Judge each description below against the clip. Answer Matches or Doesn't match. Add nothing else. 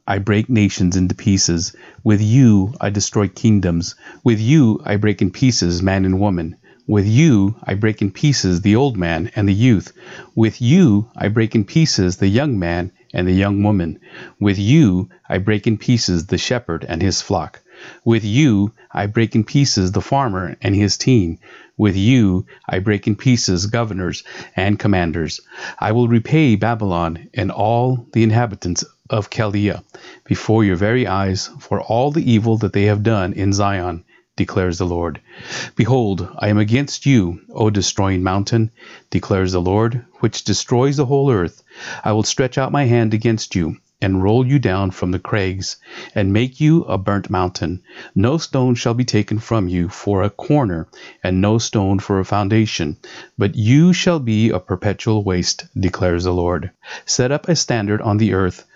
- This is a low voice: Matches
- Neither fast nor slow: Matches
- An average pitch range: Matches